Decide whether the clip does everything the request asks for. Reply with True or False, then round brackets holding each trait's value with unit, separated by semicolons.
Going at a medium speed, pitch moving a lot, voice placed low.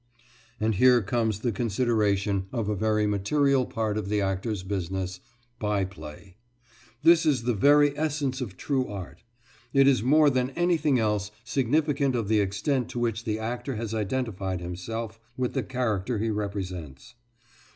False (160 wpm; 4.3 semitones; 110 Hz)